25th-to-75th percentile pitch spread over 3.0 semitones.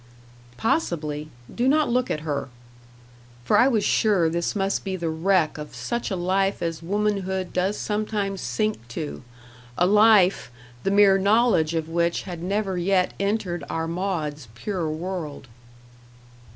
Yes: average, 3.9 semitones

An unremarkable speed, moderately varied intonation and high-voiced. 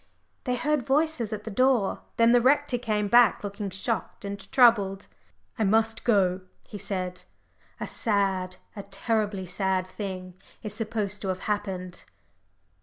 Yes: average, 150 wpm; average, 3.2 semitones; high, 205 Hz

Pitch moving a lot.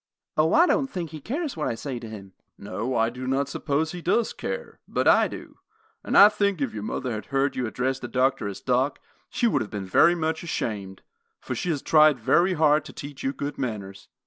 Yes: wide, 5.9 semitones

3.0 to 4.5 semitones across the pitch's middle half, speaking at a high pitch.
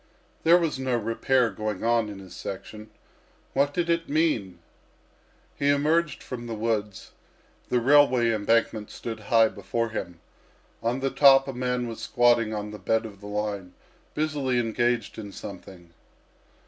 No: average, 4.1 semitones; low, 115 Hz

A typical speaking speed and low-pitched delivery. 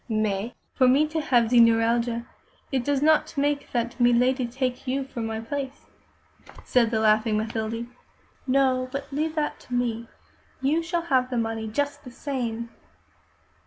No: average, 160 wpm; very high, 250 Hz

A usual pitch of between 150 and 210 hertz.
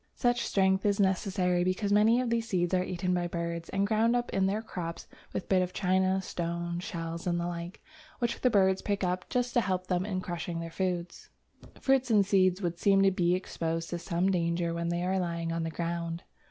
Yes: medium, 185 Hz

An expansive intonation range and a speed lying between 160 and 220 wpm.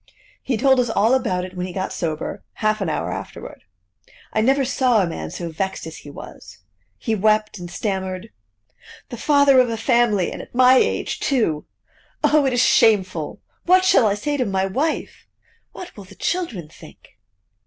Yes: wide, 5.7 semitones; average, 185 wpm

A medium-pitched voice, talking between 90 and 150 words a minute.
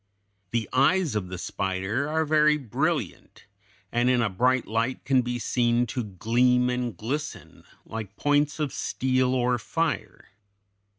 No: low, 125 Hz; average, 140 wpm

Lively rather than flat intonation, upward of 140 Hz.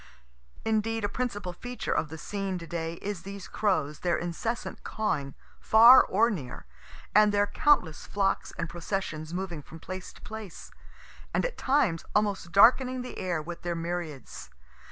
No: average, 4.5 semitones; high, 190 Hz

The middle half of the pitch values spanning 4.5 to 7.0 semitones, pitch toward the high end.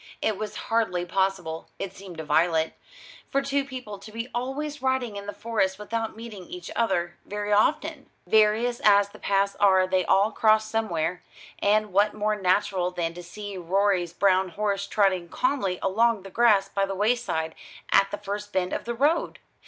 No: average, 3.2 semitones; high, 200 Hz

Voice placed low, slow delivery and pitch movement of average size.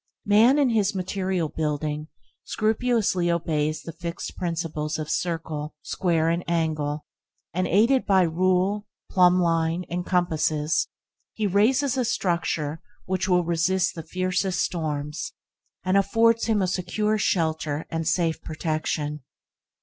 No: medium, 175 Hz; slow, 125 wpm; average, 3.4 semitones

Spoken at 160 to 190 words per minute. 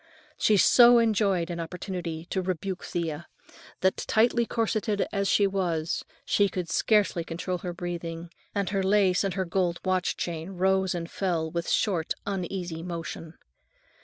No: average, 150 wpm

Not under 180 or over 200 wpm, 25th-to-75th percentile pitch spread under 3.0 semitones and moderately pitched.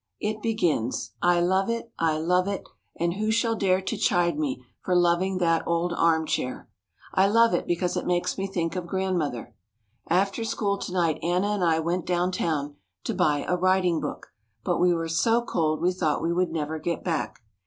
Yes: average, 195 wpm; narrow, 2.6 semitones; medium, 175 Hz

